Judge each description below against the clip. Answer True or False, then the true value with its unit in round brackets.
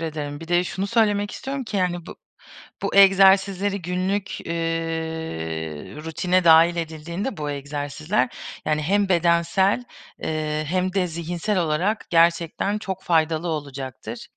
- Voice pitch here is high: False (170 Hz)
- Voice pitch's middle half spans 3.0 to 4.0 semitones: True (3.5 semitones)